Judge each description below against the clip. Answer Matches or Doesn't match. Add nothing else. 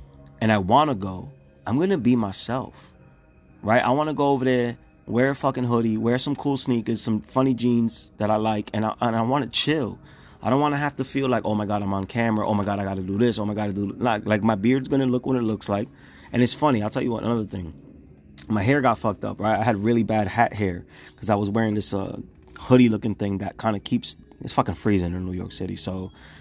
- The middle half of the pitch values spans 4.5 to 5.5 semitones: Doesn't match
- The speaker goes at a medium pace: Doesn't match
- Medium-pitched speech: Doesn't match